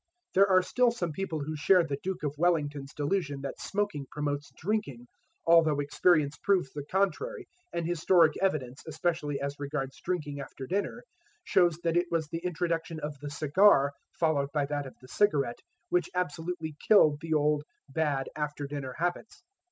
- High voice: No, medium, 155 Hz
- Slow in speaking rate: No, average, 165 wpm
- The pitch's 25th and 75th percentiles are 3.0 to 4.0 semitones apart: Yes, average, 3.7 semitones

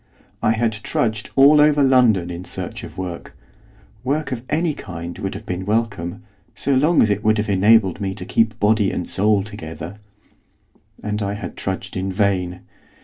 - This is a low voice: Yes, low, 105 Hz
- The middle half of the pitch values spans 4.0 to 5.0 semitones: No, average, 3.6 semitones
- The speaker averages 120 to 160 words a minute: No, average, 175 wpm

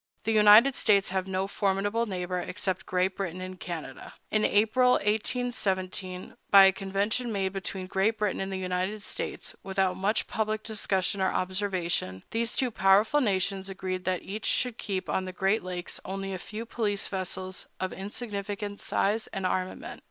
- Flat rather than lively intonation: Yes, narrow, 2.2 semitones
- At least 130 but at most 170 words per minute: Yes, average, 165 wpm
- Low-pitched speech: No, high, 195 Hz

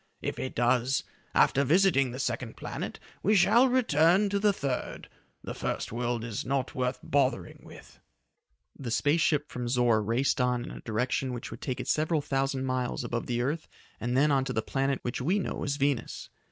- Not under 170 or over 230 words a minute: Yes, average, 195 wpm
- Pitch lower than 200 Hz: Yes, low, 135 Hz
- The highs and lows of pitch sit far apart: No, average, 3.4 semitones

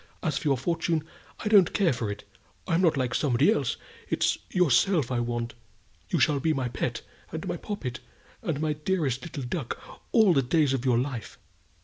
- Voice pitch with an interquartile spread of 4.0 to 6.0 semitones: Yes, average, 5.1 semitones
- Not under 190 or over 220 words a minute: Yes, average, 195 wpm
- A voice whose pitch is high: No, medium, 145 Hz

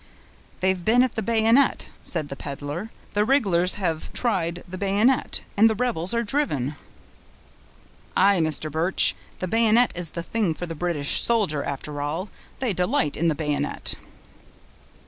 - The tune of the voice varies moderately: No, wide, 5.9 semitones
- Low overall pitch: No, medium, 180 Hz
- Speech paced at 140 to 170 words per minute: Yes, average, 150 wpm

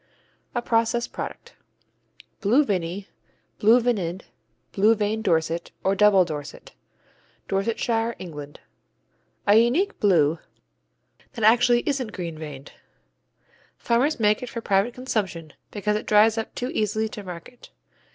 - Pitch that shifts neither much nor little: Yes, average, 4.5 semitones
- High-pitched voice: Yes, high, 210 Hz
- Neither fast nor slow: No, slow, 125 wpm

